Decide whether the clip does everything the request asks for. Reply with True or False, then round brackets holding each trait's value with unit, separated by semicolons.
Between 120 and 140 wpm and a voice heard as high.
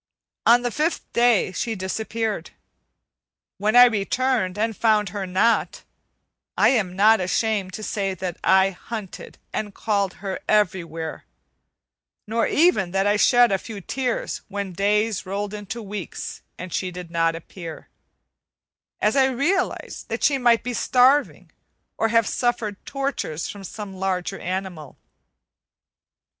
True (135 wpm; 205 Hz)